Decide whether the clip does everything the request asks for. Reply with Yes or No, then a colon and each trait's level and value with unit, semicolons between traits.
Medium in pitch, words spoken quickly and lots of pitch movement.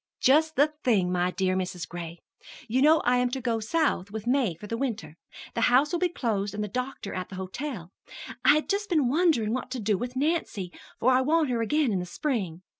No: high, 240 Hz; fast, 225 wpm; wide, 6.9 semitones